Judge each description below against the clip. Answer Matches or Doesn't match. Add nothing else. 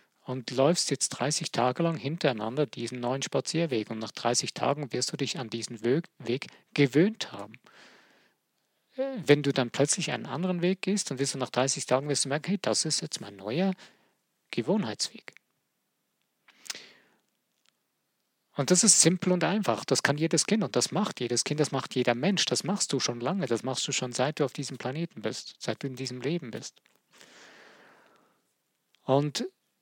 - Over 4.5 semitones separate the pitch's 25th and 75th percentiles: Matches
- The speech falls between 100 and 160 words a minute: Doesn't match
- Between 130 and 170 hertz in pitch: Matches